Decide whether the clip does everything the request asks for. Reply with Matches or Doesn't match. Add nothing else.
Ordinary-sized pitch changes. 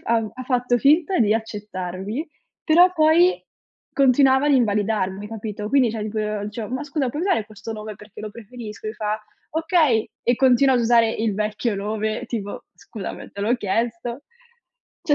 Matches